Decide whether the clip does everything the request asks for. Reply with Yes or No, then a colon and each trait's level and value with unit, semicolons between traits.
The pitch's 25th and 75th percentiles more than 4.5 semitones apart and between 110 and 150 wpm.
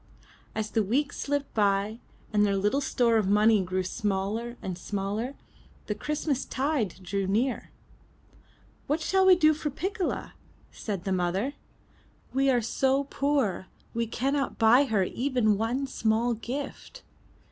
Yes: average, 5.2 semitones; average, 140 wpm